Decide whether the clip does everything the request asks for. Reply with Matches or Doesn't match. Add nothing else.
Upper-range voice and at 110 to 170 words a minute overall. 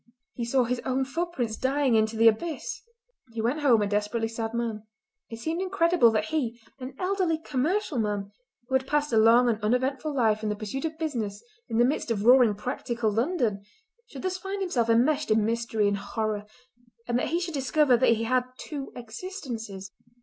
Doesn't match